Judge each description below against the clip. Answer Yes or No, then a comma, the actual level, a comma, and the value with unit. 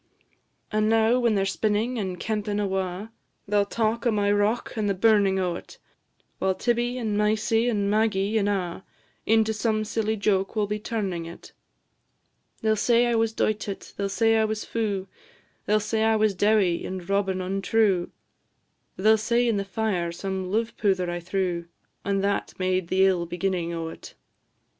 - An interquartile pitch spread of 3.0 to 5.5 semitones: No, narrow, 2.6 semitones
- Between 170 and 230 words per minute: Yes, average, 180 wpm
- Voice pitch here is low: No, high, 205 Hz